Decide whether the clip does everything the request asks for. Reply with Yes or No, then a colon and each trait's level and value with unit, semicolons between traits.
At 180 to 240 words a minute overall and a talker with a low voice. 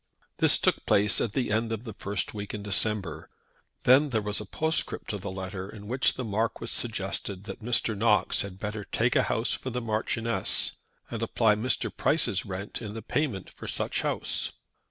Yes: average, 190 wpm; low, 105 Hz